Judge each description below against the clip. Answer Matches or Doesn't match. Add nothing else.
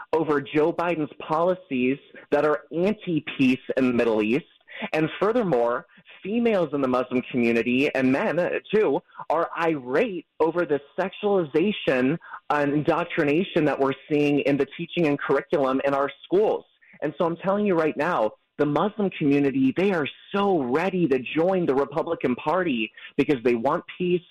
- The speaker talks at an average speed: Matches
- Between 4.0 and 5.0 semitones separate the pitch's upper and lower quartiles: Matches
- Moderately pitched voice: Matches